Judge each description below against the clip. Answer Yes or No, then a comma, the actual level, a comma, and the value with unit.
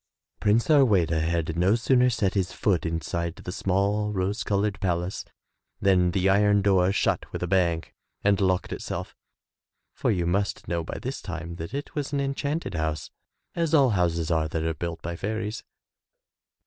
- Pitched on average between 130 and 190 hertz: No, very low, 95 Hz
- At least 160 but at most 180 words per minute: Yes, average, 170 wpm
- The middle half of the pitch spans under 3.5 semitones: No, average, 3.8 semitones